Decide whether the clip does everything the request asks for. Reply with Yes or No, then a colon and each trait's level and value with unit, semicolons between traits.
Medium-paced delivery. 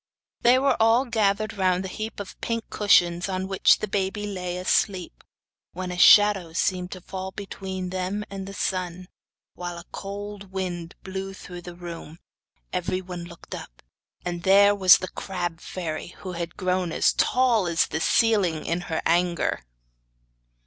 Yes: average, 160 wpm